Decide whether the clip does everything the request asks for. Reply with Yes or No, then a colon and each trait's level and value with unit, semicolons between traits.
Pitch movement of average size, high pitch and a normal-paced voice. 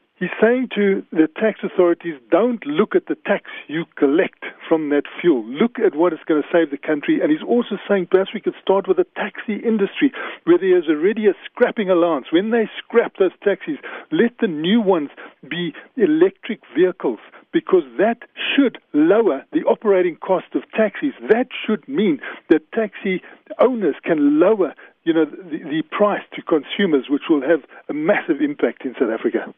No: wide, 8.3 semitones; high, 225 Hz; average, 180 wpm